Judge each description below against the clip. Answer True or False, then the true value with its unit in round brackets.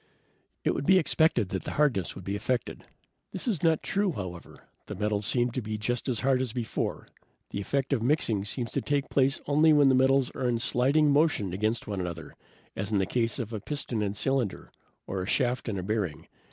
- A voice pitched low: True (120 Hz)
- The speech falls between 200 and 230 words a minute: True (205 wpm)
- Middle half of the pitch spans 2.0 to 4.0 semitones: False (5.1 semitones)